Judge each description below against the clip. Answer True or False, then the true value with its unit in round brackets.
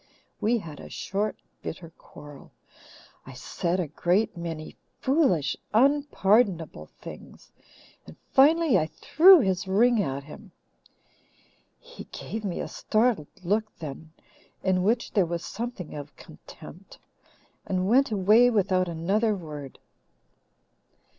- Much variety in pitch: True (5.8 semitones)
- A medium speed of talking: False (120 wpm)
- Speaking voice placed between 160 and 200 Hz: True (190 Hz)